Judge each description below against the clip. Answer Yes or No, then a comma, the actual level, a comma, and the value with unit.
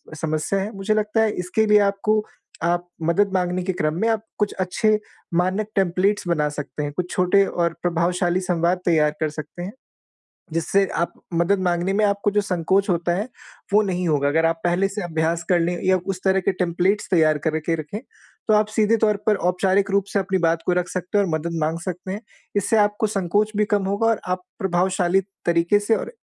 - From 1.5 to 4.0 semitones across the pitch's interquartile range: Yes, average, 3.0 semitones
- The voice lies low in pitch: No, medium, 185 Hz